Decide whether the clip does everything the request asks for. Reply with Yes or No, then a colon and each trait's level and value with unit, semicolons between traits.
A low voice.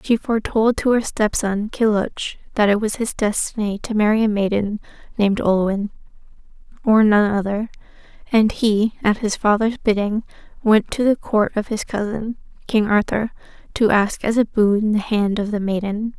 No: high, 215 Hz